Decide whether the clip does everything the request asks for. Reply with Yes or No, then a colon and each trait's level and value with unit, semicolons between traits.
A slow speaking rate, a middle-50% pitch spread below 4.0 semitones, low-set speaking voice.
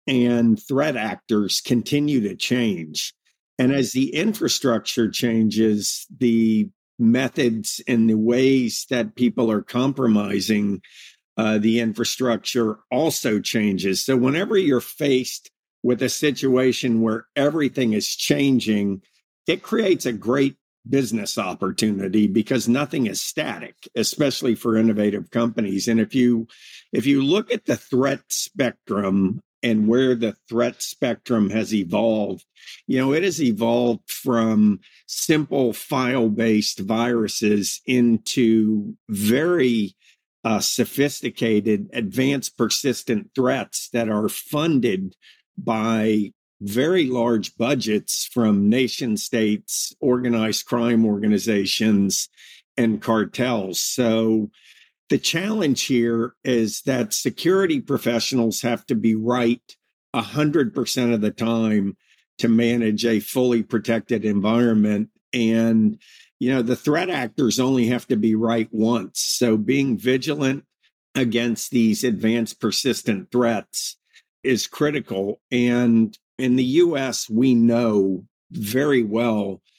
Yes: slow, 115 wpm; average, 2.7 semitones; low, 115 Hz